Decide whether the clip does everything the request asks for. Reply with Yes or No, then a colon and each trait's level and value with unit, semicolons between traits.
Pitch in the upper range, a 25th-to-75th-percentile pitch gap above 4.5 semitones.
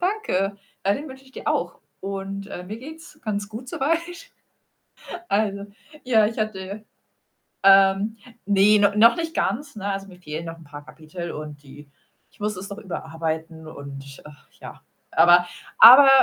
Yes: high, 200 Hz; average, 5.2 semitones